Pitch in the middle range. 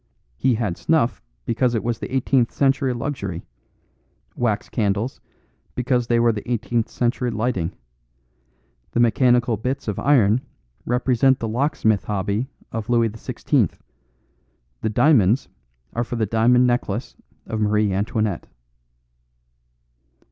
No: low, 115 Hz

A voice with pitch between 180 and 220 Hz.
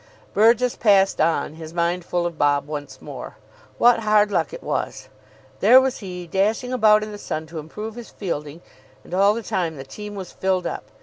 Yes: high, 190 Hz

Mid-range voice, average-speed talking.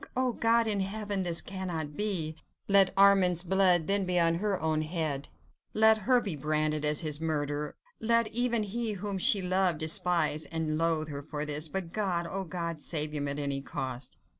Yes: medium, 170 Hz; average, 185 wpm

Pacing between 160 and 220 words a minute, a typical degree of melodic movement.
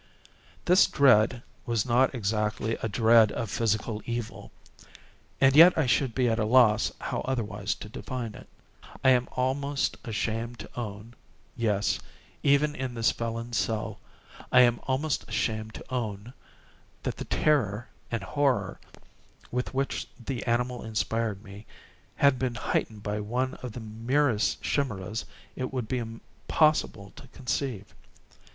No: slow, 135 wpm; average, 3.2 semitones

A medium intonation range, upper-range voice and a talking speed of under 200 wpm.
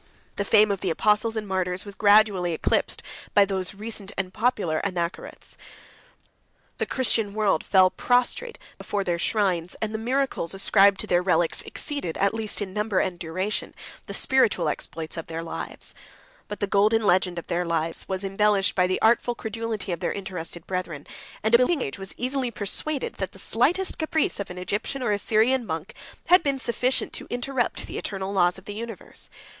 Yes: average, 3.7 semitones; high, 200 Hz; average, 185 wpm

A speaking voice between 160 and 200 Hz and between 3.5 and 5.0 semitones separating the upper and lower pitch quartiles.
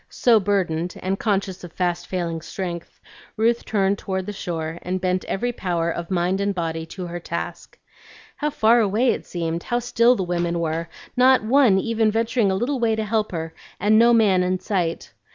Yes: high, 190 Hz; average, 4.4 semitones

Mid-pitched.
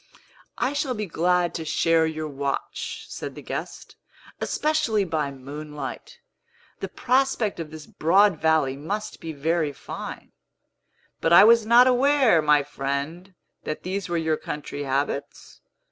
Yes: medium, 165 Hz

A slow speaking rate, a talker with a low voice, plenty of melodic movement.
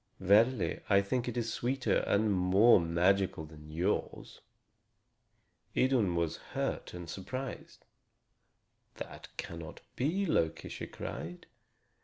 Yes: slow, 110 wpm; low, 100 Hz; wide, 6.1 semitones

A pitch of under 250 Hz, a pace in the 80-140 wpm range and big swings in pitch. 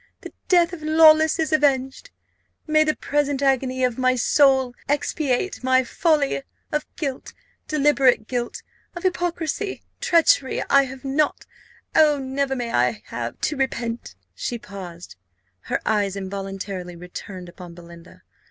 No: very high, 265 Hz; slow, 135 wpm; wide, 6.7 semitones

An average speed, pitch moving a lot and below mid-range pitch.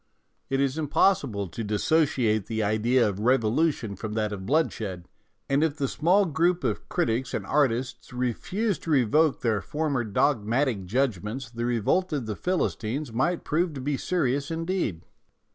Yes: average, 155 wpm; wide, 6.1 semitones; low, 130 Hz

